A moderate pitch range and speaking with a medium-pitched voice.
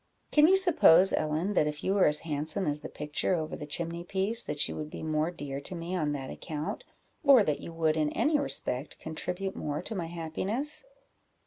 Yes: average, 4.3 semitones; medium, 165 Hz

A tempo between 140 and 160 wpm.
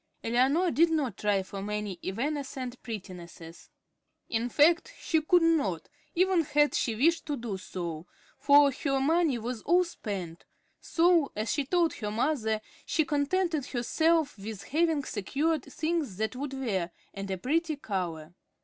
Yes: average, 150 wpm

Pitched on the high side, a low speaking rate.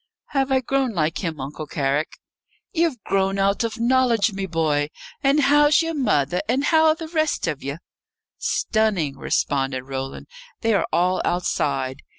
No: high, 195 Hz; average, 160 wpm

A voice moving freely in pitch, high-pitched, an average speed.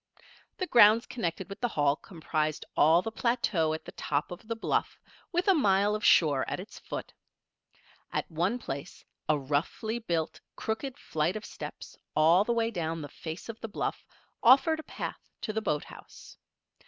Yes: wide, 6.4 semitones; high, 195 Hz; average, 175 wpm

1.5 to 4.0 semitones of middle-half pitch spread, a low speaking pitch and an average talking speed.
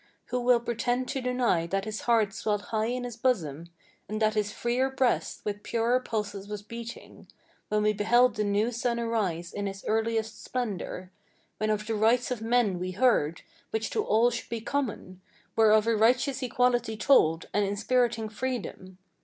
No: average, 2.8 semitones; high, 225 Hz; average, 180 wpm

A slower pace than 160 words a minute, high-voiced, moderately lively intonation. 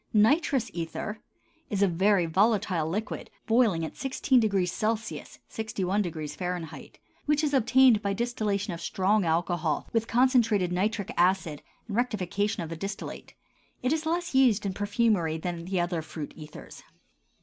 Yes: average, 140 wpm; high, 200 Hz; average, 4.6 semitones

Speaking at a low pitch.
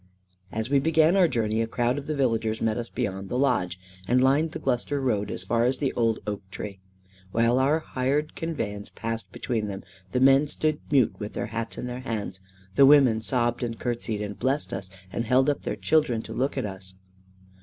Yes: low, 120 Hz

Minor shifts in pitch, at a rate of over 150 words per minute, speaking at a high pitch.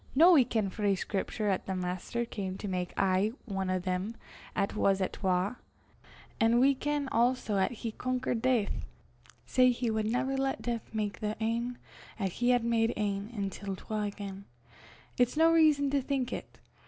No: average, 4.2 semitones; average, 180 wpm; high, 220 Hz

